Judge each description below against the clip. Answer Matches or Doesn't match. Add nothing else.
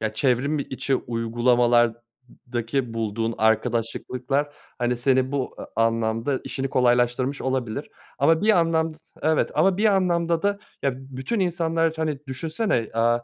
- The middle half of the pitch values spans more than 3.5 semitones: Matches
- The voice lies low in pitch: Matches